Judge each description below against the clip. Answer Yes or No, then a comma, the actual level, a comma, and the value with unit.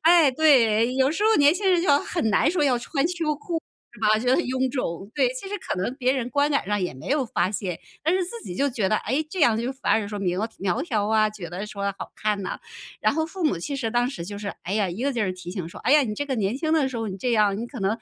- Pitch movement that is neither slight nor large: No, wide, 6.2 semitones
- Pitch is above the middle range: Yes, high, 240 Hz